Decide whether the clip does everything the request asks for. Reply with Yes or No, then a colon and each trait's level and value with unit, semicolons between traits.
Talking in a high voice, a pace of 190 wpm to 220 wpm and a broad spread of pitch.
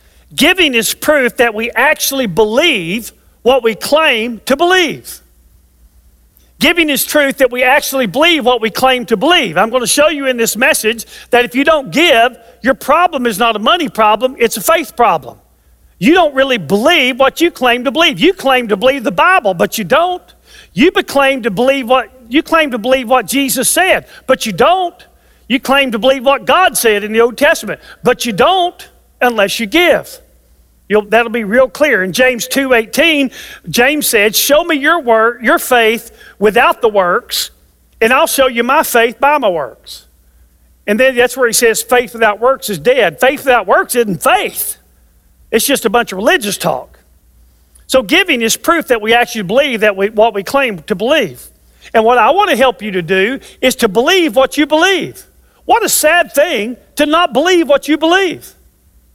No: very high, 255 Hz; average, 195 wpm; average, 4.8 semitones